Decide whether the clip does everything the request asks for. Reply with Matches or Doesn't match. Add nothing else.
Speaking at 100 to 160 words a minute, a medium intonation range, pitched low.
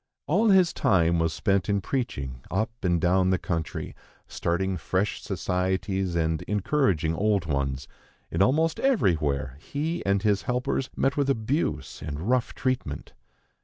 Doesn't match